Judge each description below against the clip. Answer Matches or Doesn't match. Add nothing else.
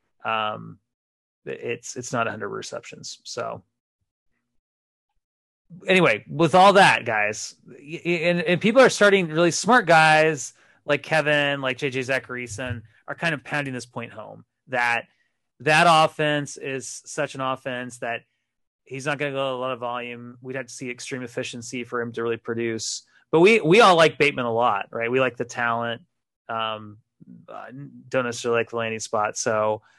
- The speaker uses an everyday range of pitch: Matches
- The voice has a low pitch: Matches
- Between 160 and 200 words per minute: Matches